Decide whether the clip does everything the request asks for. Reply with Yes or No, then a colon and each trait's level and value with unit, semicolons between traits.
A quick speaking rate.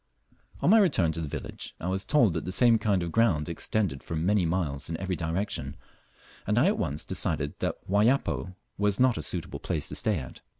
Yes: fast, 210 wpm